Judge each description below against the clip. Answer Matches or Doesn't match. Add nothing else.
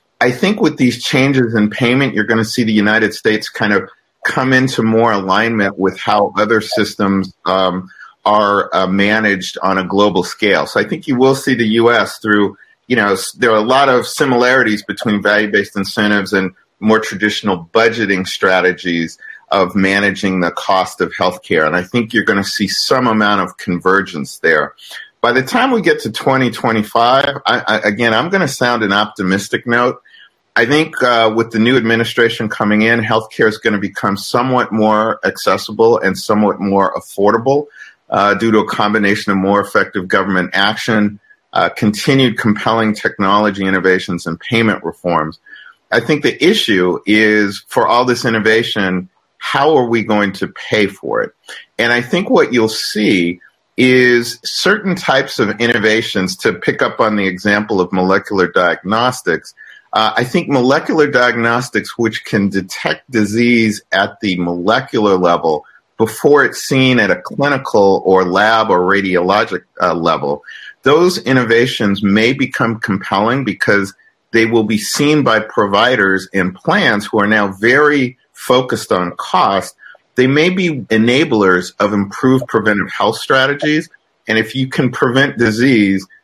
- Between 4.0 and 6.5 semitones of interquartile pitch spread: Doesn't match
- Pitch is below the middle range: Matches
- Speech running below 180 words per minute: Matches